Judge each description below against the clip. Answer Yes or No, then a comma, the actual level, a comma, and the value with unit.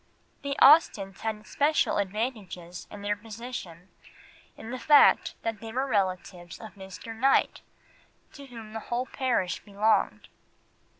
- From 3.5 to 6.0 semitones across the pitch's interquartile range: Yes, average, 4.4 semitones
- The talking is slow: Yes, slow, 130 wpm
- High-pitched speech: Yes, high, 220 Hz